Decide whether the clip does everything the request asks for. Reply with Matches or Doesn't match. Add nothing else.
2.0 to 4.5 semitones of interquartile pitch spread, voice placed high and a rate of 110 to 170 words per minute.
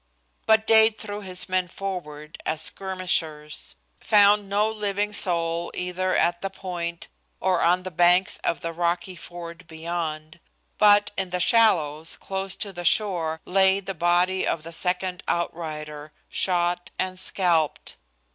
Doesn't match